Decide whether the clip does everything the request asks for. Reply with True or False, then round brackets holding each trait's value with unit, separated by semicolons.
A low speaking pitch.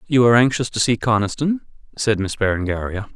True (115 Hz)